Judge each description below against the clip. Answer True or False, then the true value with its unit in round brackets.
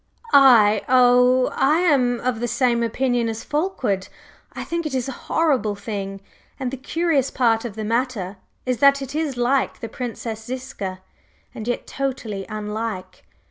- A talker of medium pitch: False (245 Hz)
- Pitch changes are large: False (3.5 semitones)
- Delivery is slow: False (160 wpm)